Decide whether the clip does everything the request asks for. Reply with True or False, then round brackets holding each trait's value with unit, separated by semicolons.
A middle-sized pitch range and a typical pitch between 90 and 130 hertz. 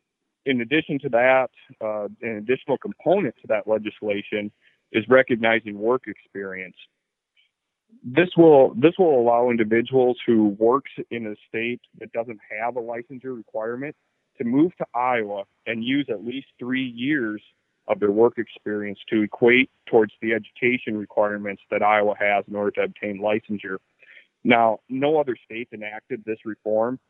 True (3.4 semitones; 115 Hz)